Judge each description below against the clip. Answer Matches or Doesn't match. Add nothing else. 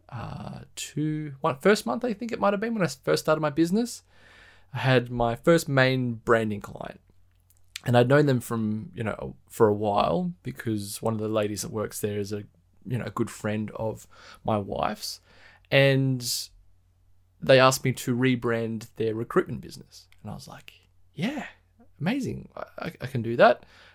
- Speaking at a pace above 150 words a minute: Matches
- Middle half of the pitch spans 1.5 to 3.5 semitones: Doesn't match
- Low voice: Matches